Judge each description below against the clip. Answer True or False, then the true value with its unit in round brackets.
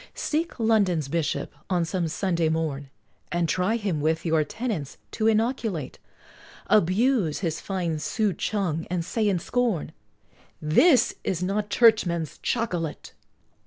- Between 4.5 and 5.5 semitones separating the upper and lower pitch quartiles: True (5.2 semitones)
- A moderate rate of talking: False (125 wpm)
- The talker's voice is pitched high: False (180 Hz)